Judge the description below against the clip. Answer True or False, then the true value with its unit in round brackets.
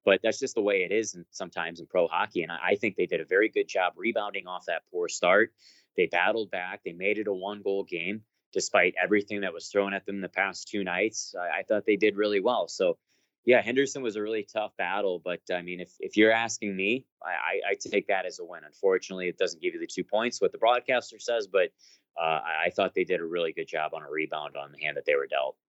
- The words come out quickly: True (250 wpm)